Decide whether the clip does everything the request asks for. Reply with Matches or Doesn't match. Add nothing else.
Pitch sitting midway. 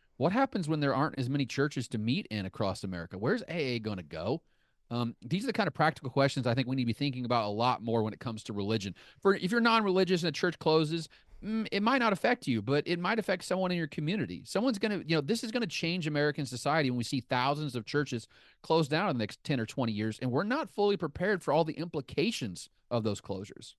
Matches